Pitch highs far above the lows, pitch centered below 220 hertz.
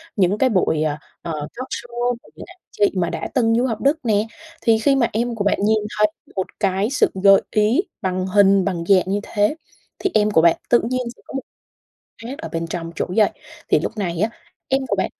No: average, 4.3 semitones; high, 210 Hz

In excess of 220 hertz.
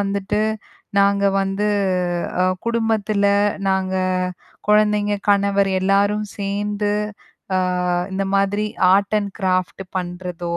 No: high, 200 Hz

